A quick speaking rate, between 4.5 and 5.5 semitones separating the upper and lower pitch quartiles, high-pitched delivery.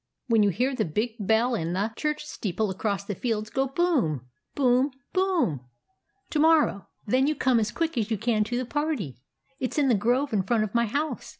Yes: fast, 210 wpm; average, 5.2 semitones; high, 235 Hz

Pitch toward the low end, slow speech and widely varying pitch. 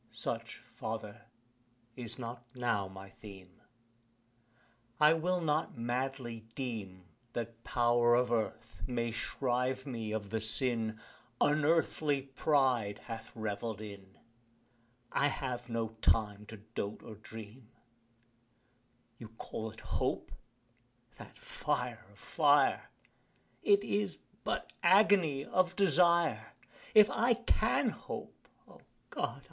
No: low, 120 Hz; slow, 110 wpm; average, 4.8 semitones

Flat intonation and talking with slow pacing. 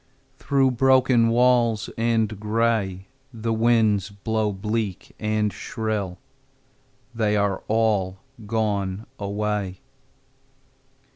Yes: narrow, 2.2 semitones; slow, 85 wpm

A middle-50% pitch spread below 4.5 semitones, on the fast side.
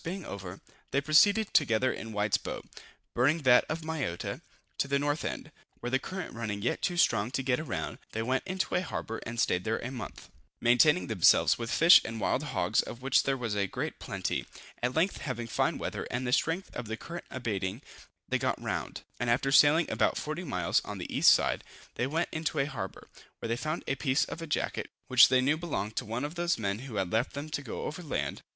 No: wide, 5.5 semitones; fast, 220 wpm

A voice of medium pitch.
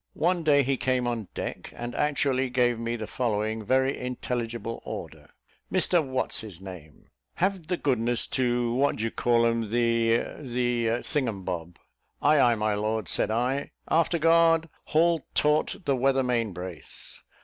No: low, 120 Hz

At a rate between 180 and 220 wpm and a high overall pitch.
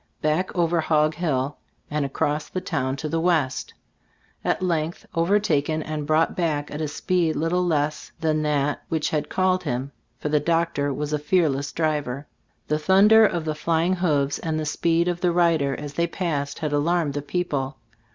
No: average, 185 wpm; medium, 155 Hz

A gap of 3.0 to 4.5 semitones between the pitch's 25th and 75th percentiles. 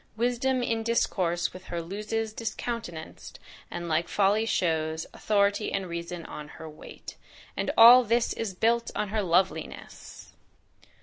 No: average, 5.0 semitones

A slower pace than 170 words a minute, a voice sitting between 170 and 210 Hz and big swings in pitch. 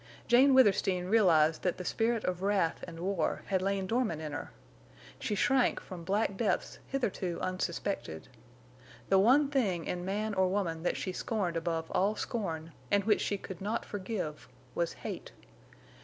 No: average, 160 wpm; high, 190 Hz; average, 3.9 semitones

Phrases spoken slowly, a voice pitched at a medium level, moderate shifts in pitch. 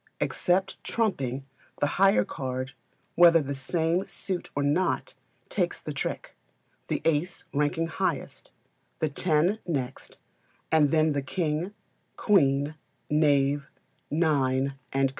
Yes: slow, 120 wpm; medium, 150 Hz; average, 3.9 semitones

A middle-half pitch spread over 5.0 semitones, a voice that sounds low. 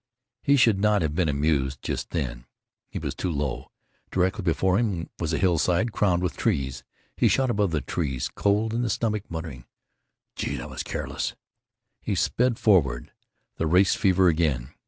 Yes: wide, 5.6 semitones; very low, 90 Hz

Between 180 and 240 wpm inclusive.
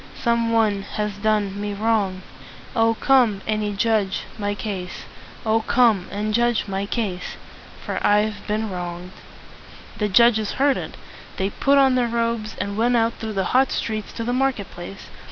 No: average, 165 wpm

